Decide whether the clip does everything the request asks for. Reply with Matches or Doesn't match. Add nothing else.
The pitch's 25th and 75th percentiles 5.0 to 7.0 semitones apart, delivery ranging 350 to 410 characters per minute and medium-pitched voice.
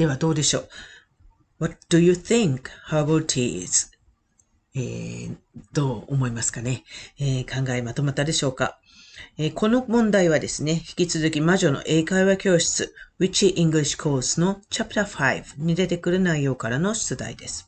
Doesn't match